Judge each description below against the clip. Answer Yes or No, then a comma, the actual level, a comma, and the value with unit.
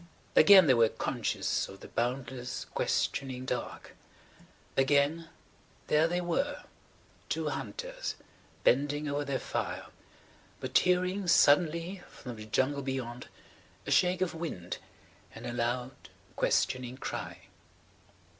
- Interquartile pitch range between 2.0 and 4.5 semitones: No, wide, 5.6 semitones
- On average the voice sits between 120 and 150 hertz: Yes, medium, 140 Hz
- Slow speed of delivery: Yes, slow, 115 wpm